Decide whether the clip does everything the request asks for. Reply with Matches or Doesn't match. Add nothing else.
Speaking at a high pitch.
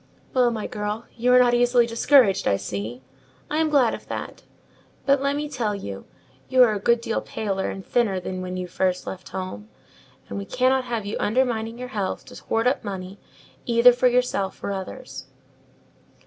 Matches